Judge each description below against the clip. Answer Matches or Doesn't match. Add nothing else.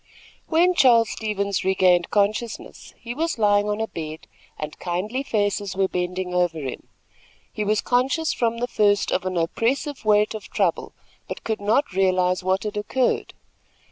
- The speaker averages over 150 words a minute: Matches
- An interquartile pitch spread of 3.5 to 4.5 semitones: Matches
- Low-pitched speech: Doesn't match